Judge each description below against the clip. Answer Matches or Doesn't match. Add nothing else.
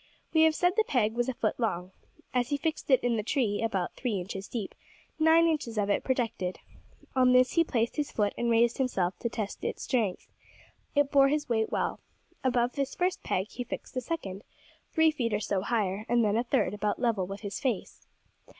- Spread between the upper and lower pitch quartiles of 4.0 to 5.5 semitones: Matches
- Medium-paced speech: Doesn't match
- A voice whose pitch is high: Matches